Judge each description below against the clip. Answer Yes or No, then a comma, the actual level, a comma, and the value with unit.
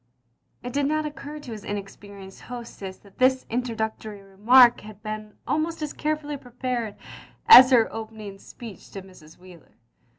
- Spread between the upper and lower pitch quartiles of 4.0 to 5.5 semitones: Yes, average, 4.3 semitones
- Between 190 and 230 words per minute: No, average, 160 wpm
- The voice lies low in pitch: No, high, 225 Hz